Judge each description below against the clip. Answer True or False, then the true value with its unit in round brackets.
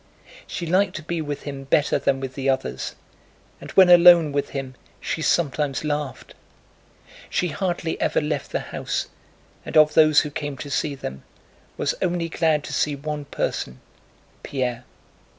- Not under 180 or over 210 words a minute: False (160 wpm)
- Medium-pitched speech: True (150 Hz)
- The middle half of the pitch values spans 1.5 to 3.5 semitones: True (2.6 semitones)